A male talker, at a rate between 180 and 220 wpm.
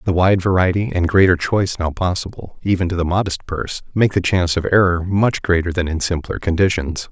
Yes: male; average, 200 wpm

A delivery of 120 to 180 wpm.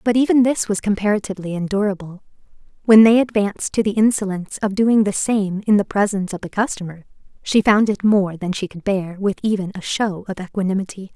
No: average, 195 wpm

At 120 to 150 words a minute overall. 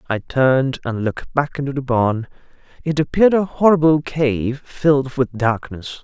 No: average, 160 wpm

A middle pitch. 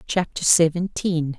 Yes: medium, 165 Hz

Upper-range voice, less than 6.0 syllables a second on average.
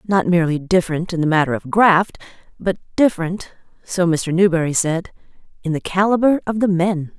No: medium, 180 Hz; 5.5 syllables/s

